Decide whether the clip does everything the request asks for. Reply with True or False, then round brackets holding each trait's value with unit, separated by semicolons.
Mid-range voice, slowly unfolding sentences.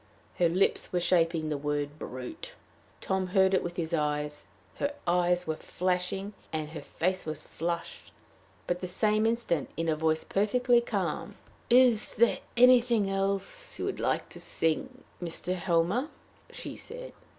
False (180 Hz; 150 wpm)